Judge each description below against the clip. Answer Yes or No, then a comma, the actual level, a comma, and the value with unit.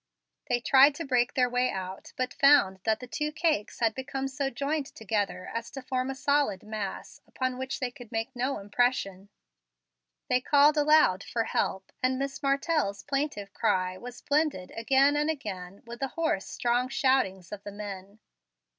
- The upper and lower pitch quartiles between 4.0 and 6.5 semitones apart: Yes, average, 5.2 semitones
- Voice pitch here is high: Yes, very high, 250 Hz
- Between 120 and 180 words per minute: Yes, average, 170 wpm